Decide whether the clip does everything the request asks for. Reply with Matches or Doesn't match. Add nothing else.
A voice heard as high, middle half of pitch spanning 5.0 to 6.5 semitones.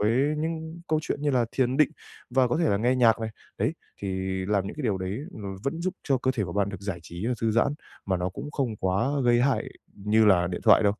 Doesn't match